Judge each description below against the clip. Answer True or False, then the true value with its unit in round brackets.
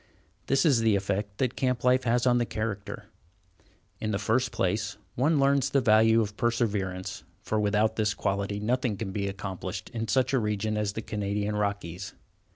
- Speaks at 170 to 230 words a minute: True (175 wpm)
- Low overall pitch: True (110 Hz)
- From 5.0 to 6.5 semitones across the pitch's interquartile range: False (3.1 semitones)